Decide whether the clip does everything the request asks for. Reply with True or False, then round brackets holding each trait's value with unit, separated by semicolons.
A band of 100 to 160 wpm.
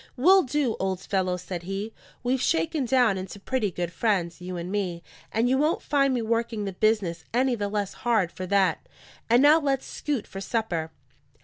False (190 wpm)